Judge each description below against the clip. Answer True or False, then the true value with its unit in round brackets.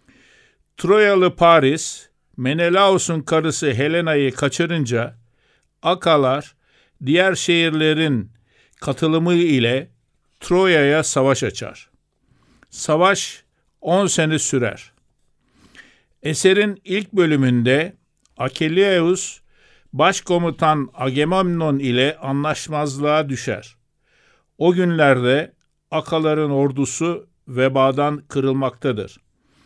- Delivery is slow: True (65 wpm)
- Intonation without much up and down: False (4.2 semitones)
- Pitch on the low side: False (150 Hz)